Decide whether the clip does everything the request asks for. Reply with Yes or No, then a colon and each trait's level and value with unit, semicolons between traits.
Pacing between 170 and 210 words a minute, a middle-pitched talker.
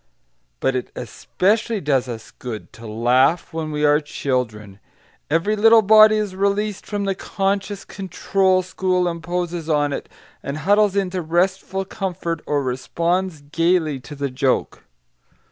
No: average, 140 wpm; medium, 170 Hz